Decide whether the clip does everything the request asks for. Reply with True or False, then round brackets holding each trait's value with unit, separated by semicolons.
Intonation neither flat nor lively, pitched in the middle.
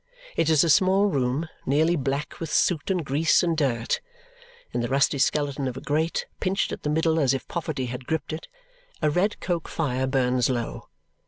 True (3.7 semitones; 150 Hz)